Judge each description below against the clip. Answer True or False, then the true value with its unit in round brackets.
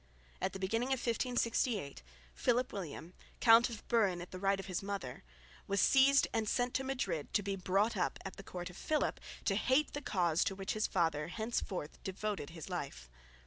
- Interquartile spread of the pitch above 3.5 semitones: True (4.6 semitones)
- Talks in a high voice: True (200 Hz)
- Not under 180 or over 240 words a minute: True (185 wpm)